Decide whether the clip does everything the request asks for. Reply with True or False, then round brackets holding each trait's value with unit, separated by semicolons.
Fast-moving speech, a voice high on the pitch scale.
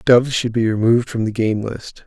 False (235 wpm; 115 Hz)